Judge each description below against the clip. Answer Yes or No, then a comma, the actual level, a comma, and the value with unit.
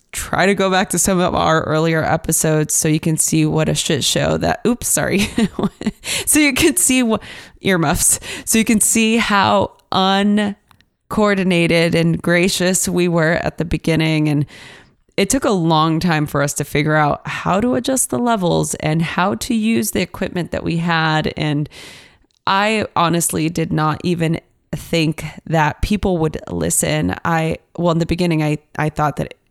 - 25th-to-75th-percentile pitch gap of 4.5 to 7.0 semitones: No, average, 3.8 semitones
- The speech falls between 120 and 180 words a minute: Yes, average, 175 wpm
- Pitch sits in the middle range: Yes, medium, 170 Hz